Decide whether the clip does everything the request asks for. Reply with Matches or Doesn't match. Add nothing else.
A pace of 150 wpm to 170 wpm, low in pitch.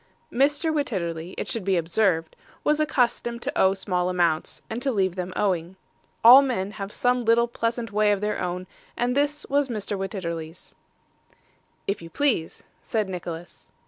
Doesn't match